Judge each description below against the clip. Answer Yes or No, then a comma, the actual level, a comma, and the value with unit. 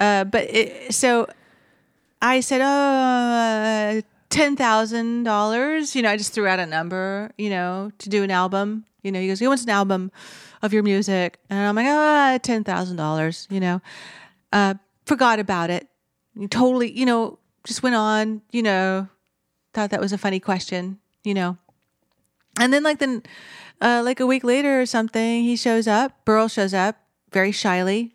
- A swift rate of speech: No, average, 170 wpm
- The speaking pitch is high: Yes, high, 215 Hz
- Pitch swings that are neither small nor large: Yes, average, 3.7 semitones